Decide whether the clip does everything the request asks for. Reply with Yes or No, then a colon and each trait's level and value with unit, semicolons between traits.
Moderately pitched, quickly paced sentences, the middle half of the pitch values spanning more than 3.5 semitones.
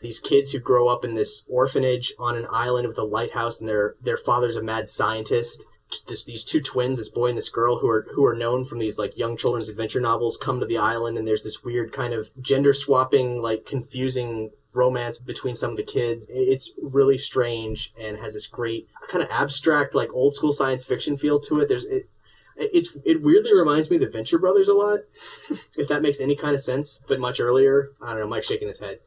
No: low, 130 Hz; fast, 225 wpm; average, 4.2 semitones